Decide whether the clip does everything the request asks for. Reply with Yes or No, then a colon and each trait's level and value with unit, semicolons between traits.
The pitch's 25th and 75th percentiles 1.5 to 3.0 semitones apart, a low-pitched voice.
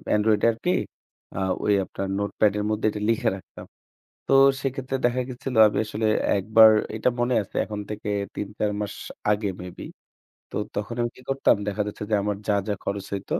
Yes: narrow, 2.4 semitones; low, 105 Hz